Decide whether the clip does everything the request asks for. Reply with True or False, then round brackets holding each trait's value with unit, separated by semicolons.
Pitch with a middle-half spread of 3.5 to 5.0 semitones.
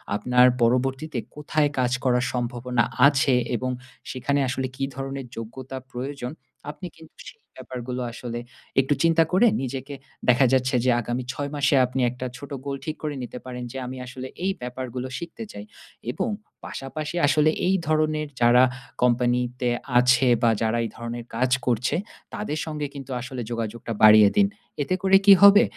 False (2.8 semitones)